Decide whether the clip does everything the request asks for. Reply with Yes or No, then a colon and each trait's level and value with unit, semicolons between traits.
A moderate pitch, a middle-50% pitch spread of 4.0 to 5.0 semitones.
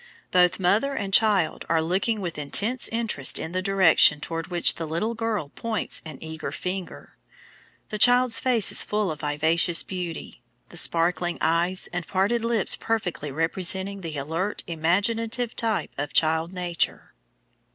Yes: medium, 180 Hz; average, 4.7 semitones